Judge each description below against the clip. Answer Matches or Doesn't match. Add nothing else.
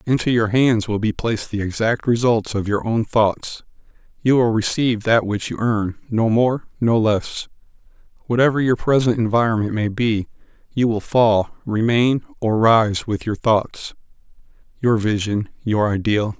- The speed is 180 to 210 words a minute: Doesn't match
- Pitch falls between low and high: Doesn't match